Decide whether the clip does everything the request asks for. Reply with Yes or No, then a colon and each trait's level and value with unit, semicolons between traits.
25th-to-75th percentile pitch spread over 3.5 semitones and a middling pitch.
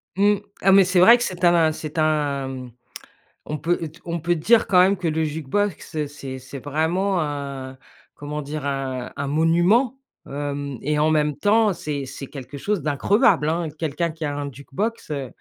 Yes: average, 3.9 semitones; medium, 155 Hz